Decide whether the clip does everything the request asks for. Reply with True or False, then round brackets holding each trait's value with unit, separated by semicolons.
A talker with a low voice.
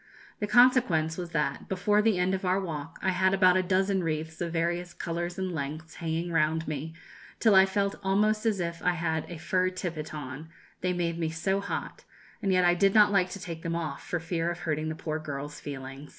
False (175 Hz)